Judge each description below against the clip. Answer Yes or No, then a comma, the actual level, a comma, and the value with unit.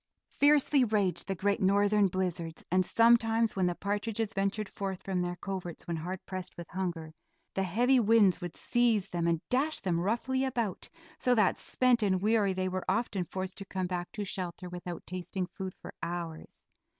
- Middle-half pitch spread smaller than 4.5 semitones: Yes, average, 3.7 semitones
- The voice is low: No, high, 190 Hz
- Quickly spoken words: No, average, 180 wpm